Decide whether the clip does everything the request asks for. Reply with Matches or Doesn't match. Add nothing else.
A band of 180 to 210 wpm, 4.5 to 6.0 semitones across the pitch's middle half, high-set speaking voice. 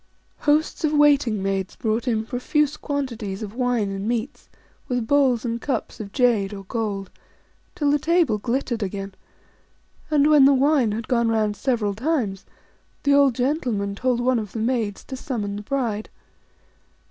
Doesn't match